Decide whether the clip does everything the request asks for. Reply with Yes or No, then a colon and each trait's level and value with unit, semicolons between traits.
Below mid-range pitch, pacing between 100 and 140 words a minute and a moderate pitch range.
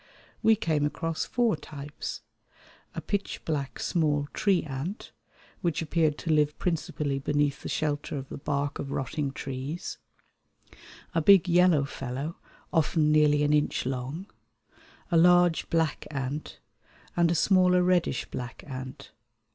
No: medium, 150 Hz; slow, 135 wpm; average, 3.3 semitones